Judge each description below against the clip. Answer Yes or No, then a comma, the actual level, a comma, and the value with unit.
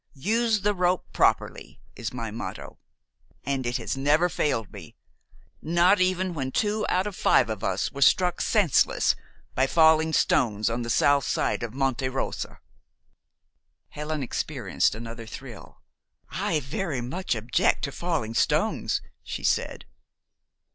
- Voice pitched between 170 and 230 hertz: No, medium, 140 Hz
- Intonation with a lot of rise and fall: Yes, wide, 6.8 semitones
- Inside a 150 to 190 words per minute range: No, average, 140 wpm